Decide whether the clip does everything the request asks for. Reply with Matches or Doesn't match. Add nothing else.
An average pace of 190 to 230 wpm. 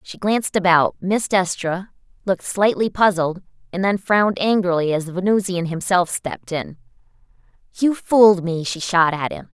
Doesn't match